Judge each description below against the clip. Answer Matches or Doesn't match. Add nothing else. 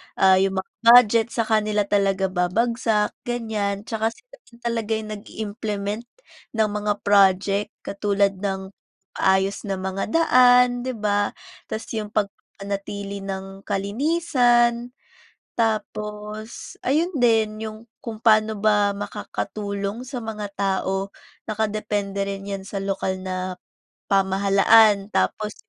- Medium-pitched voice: Doesn't match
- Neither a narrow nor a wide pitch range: Doesn't match